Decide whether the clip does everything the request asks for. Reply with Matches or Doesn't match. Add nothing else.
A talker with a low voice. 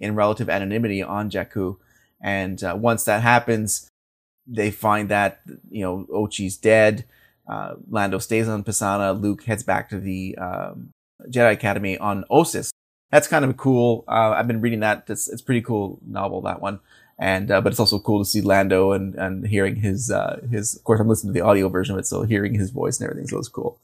Matches